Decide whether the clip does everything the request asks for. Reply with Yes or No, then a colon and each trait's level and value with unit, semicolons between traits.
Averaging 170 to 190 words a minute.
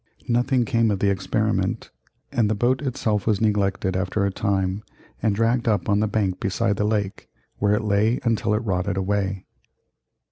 Yes: average, 175 wpm